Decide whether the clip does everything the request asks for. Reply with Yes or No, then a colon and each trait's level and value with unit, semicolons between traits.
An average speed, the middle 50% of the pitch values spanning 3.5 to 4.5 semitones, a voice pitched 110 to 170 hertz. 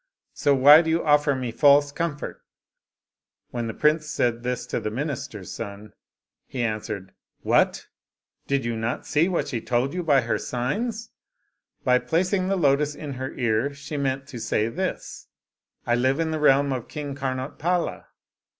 Yes: average, 170 wpm; average, 3.9 semitones; medium, 140 Hz